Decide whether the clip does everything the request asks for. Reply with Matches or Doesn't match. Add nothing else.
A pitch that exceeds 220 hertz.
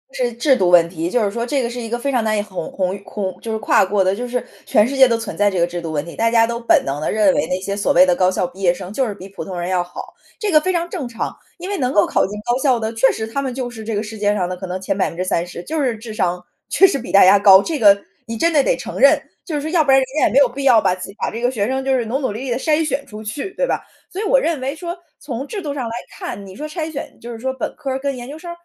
Matches